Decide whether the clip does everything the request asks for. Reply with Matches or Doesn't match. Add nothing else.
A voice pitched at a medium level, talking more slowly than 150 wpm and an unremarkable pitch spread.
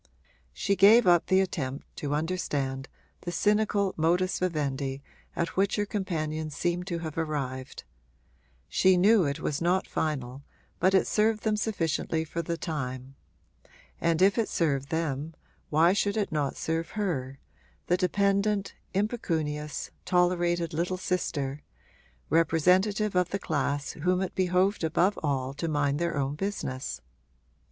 Matches